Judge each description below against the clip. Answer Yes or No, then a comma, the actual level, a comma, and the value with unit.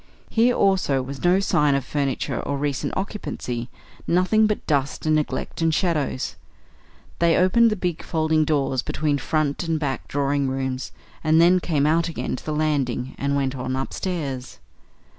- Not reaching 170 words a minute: Yes, average, 160 wpm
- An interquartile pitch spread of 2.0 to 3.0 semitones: No, average, 3.8 semitones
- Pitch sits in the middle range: Yes, medium, 150 Hz